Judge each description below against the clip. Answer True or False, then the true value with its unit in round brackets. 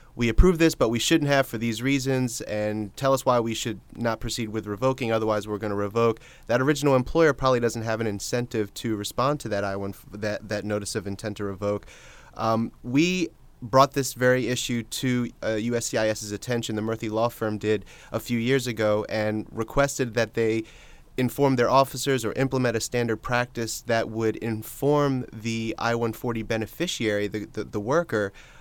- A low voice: True (115 Hz)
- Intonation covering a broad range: False (2.9 semitones)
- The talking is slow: False (185 wpm)